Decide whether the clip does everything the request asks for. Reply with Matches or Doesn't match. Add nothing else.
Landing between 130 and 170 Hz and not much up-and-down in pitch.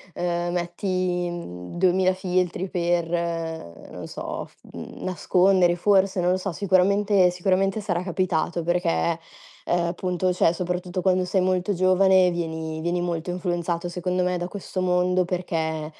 Doesn't match